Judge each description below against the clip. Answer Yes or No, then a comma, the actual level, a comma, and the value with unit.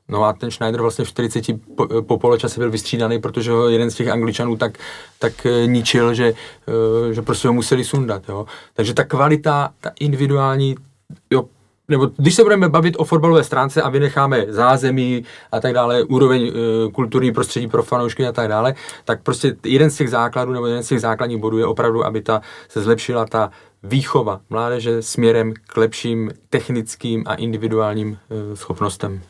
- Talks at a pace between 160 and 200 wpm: Yes, fast, 170 wpm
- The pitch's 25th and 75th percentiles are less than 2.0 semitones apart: No, average, 2.8 semitones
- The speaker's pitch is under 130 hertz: Yes, low, 120 Hz